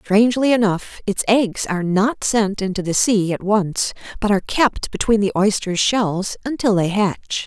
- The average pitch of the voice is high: Yes, high, 205 Hz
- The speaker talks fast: No, average, 175 wpm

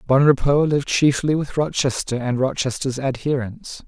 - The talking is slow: Yes, slow, 125 wpm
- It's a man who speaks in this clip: Yes, male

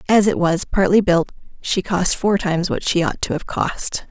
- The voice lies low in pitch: No, medium, 185 Hz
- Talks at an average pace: No, fast, 220 wpm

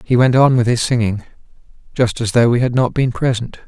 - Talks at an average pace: No, fast, 230 wpm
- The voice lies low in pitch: Yes, low, 120 Hz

